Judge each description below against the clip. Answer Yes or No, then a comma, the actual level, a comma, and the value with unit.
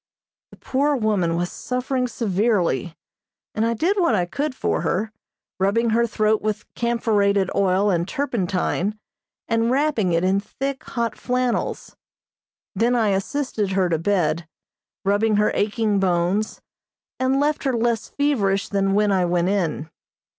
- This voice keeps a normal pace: Yes, average, 145 wpm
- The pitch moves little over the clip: No, average, 4.0 semitones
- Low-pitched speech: No, high, 210 Hz